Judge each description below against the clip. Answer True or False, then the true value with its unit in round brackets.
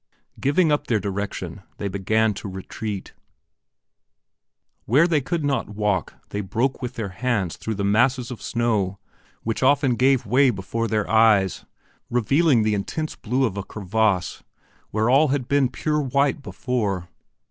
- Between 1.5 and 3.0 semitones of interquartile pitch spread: False (4.8 semitones)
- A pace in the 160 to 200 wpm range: False (150 wpm)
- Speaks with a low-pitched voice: True (115 Hz)